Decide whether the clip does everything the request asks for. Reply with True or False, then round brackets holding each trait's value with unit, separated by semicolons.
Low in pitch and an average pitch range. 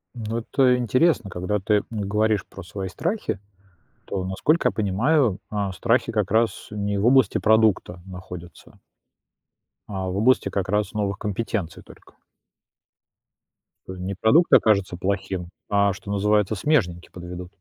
True (105 Hz; 3.2 semitones)